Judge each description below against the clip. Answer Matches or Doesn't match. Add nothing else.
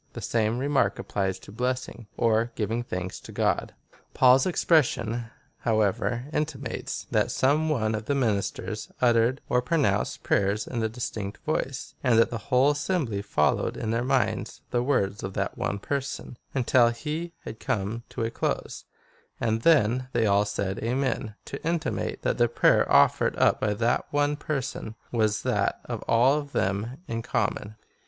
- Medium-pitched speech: Doesn't match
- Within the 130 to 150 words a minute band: Doesn't match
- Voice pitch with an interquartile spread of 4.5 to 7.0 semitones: Doesn't match